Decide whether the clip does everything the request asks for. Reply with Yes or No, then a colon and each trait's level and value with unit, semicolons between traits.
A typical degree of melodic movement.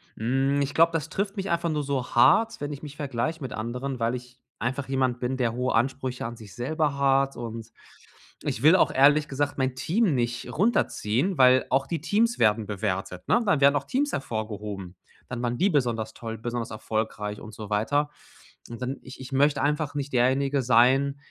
Yes: average, 3.7 semitones